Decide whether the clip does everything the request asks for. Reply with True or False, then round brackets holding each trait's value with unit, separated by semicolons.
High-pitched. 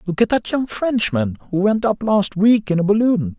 True (200 Hz)